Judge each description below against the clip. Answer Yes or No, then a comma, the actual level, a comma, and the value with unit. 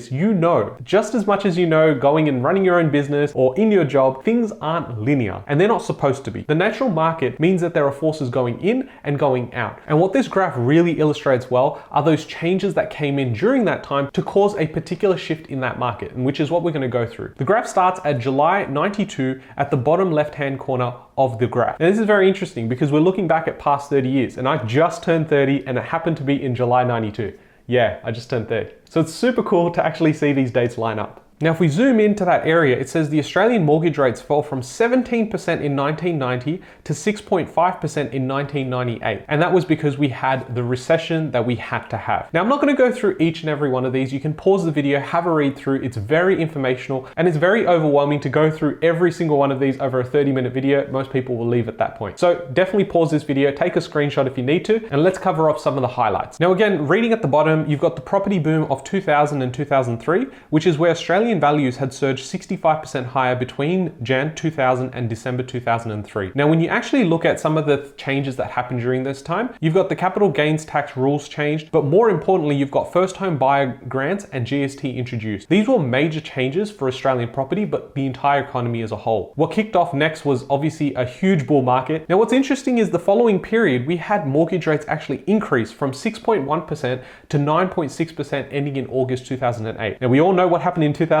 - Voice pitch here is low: No, medium, 150 Hz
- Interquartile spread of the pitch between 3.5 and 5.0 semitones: Yes, average, 4.7 semitones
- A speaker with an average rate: No, fast, 230 wpm